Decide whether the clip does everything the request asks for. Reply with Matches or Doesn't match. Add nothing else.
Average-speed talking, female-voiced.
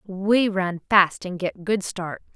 Matches